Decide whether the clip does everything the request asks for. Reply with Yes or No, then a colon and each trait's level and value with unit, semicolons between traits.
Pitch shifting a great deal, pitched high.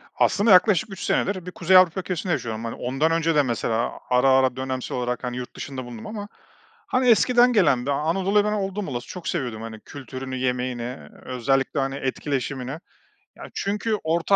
No: wide, 6.8 semitones; medium, 140 Hz